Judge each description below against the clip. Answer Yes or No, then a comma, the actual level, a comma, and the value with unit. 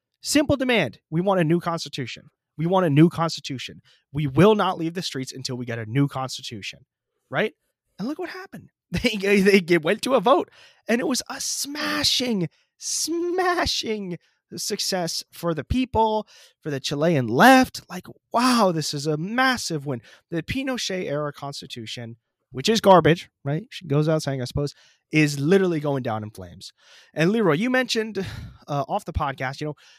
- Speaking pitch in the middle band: Yes, medium, 165 Hz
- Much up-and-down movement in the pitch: Yes, wide, 7.3 semitones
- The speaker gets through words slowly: No, average, 170 wpm